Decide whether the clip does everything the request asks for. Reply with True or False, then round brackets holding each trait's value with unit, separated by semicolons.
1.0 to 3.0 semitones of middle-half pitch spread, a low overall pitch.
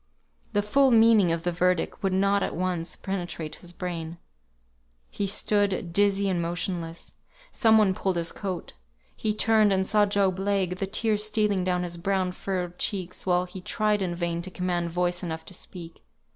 False (2.4 semitones; 185 Hz)